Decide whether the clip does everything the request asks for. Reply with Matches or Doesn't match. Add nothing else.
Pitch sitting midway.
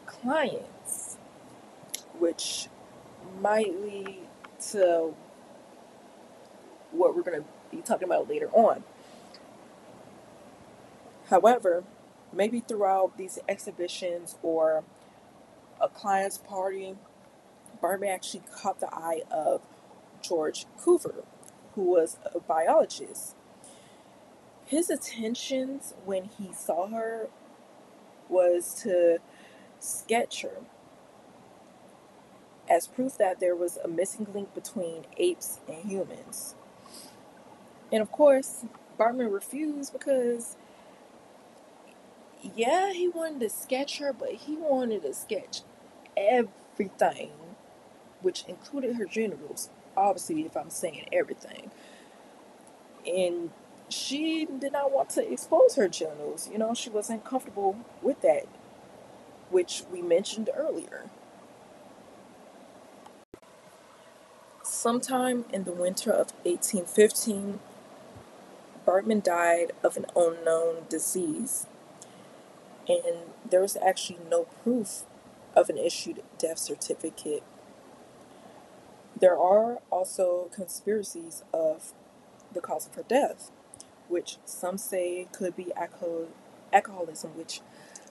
Doesn't match